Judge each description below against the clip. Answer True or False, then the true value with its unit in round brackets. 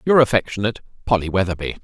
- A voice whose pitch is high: False (105 Hz)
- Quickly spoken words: False (130 wpm)